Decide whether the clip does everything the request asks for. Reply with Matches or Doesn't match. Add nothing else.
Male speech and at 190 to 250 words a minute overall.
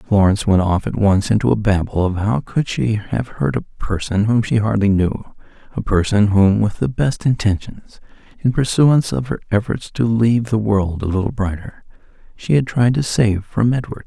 Matches